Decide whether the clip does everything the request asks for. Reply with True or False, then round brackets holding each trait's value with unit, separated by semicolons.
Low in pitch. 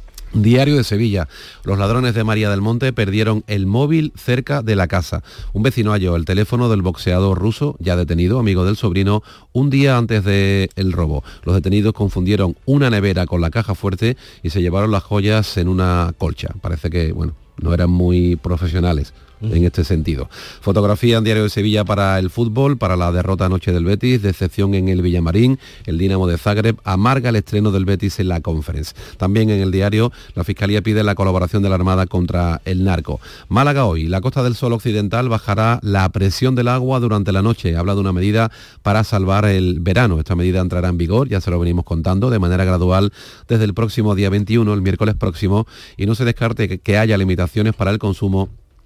True (100 Hz)